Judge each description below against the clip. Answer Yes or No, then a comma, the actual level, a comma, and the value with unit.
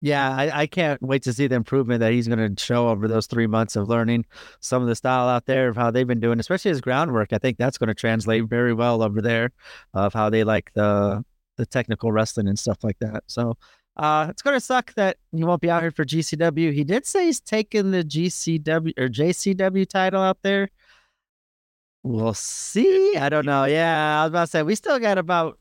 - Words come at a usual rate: No, fast, 225 wpm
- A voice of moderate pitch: No, low, 130 Hz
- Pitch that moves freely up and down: Yes, wide, 6.6 semitones